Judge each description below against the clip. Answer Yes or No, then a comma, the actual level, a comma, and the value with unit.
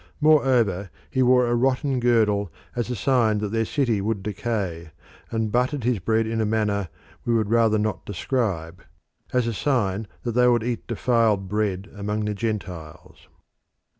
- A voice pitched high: No, low, 110 Hz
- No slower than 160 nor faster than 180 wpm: Yes, average, 165 wpm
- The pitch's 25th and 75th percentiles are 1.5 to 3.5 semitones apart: Yes, average, 3.1 semitones